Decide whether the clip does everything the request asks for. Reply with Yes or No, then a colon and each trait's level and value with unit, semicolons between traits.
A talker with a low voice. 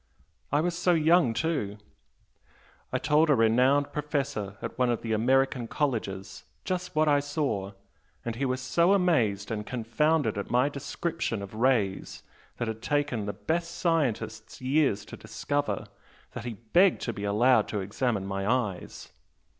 Yes: low, 125 Hz